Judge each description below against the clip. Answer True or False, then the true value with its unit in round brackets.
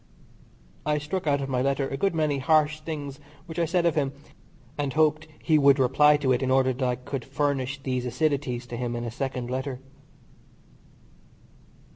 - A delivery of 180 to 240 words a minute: True (185 wpm)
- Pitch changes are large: False (2.7 semitones)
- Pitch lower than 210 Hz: True (140 Hz)